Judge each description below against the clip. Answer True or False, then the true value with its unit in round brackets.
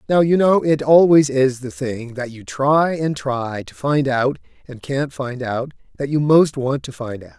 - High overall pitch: False (135 Hz)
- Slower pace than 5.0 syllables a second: True (4.2 syllables/s)